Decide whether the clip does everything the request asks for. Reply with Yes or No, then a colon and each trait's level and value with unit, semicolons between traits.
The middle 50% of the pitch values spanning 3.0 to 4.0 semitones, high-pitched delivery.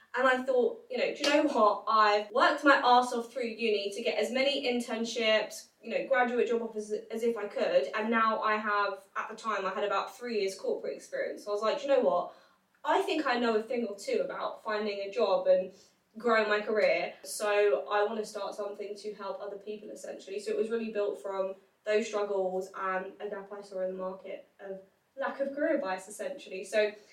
Yes: average, 3.5 semitones; high, 215 Hz